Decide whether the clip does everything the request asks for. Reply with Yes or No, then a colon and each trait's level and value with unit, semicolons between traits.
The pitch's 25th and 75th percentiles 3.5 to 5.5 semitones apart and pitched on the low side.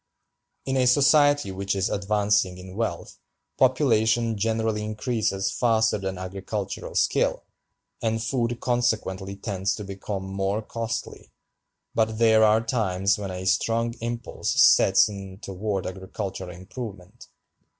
No: average, 3.0 semitones; low, 105 Hz